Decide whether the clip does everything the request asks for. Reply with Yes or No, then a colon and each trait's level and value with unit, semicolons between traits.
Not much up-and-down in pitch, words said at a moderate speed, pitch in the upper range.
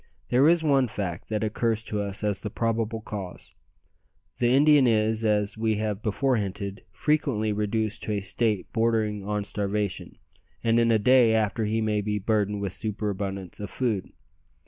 No: narrow, 1.9 semitones; average, 170 wpm; low, 110 Hz